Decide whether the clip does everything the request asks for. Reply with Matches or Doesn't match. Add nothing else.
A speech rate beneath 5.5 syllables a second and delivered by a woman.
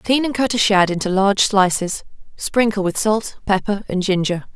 Matches